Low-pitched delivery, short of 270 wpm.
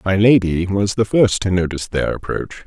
Yes: very low, 95 Hz; average, 200 wpm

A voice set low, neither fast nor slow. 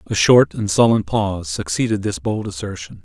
Yes: very low, 95 Hz; average, 180 wpm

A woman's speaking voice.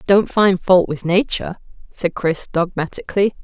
Yes: female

